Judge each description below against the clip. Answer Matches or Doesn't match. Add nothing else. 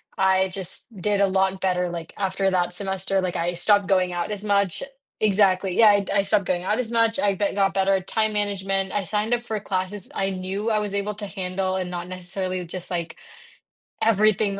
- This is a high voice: Matches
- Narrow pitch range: Matches